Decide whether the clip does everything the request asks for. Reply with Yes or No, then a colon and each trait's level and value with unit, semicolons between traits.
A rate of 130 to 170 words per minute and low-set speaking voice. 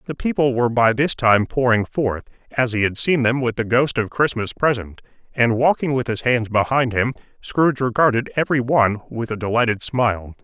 No: average, 195 wpm; low, 120 Hz